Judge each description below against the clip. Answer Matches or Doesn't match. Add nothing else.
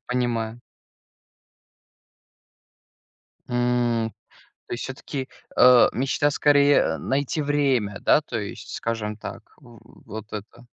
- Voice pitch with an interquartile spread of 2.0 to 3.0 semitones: Doesn't match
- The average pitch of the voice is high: Doesn't match